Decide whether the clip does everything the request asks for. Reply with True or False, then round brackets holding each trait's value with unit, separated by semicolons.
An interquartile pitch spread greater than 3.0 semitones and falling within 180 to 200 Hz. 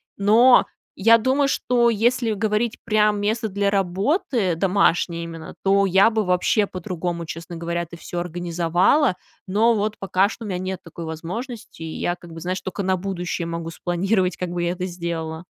True (3.7 semitones; 185 Hz)